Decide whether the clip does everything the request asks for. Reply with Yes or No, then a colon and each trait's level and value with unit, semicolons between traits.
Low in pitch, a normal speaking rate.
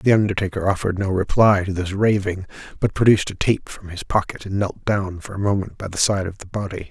No: low, 100 Hz; fast, 225 wpm